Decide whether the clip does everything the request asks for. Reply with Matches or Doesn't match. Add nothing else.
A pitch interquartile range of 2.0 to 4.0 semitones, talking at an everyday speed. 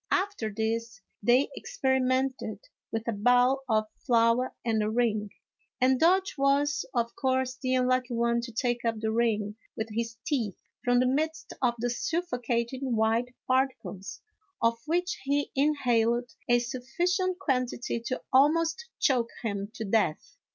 Matches